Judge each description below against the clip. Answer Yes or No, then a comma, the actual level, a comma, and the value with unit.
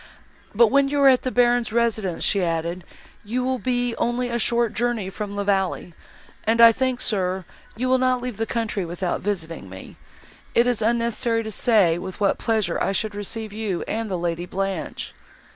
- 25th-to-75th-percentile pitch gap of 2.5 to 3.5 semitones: No, average, 4.0 semitones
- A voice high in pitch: Yes, high, 220 Hz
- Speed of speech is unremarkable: Yes, average, 190 wpm